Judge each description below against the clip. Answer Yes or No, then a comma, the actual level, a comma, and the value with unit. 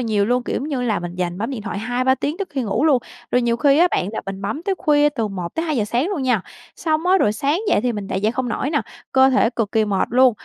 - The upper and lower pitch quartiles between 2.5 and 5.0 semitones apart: No, wide, 5.5 semitones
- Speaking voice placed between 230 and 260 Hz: Yes, high, 245 Hz